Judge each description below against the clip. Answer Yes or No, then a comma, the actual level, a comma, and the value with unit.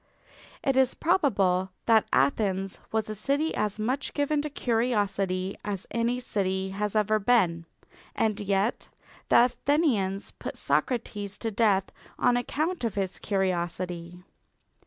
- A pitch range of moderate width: Yes, average, 4.4 semitones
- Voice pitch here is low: No, high, 210 Hz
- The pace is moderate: No, slow, 130 wpm